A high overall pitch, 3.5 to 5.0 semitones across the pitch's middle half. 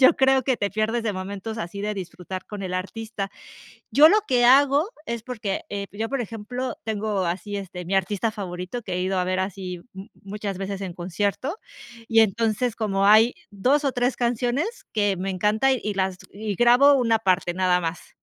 Yes: high, 210 Hz; average, 4.1 semitones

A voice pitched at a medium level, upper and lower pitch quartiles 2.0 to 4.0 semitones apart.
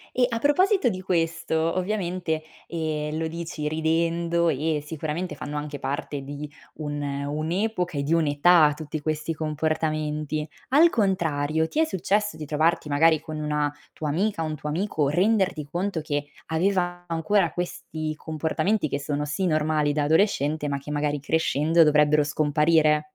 Yes: medium, 155 Hz; narrow, 2.5 semitones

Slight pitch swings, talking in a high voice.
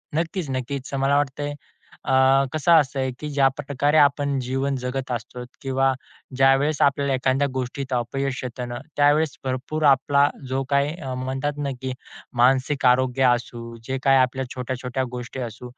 No: narrow, 1.7 semitones; low, 135 Hz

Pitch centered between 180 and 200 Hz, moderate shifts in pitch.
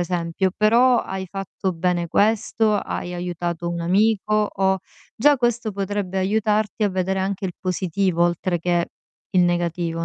Yes: high, 190 Hz; average, 3.1 semitones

